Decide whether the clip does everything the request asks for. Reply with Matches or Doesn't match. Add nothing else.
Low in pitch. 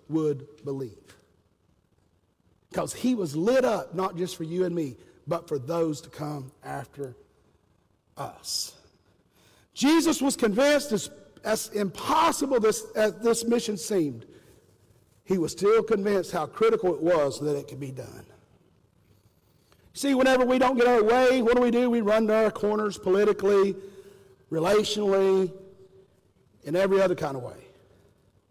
Doesn't match